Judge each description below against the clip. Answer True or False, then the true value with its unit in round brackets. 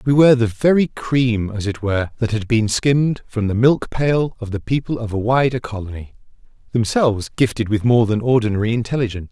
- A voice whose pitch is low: True (115 Hz)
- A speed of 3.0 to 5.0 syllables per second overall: False (5.8 syllables/s)